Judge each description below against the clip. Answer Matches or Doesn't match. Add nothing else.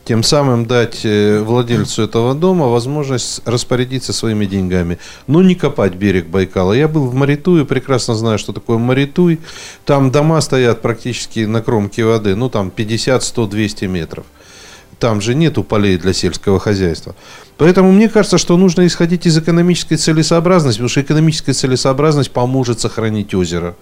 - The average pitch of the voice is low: Matches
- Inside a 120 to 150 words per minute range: Matches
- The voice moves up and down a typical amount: Doesn't match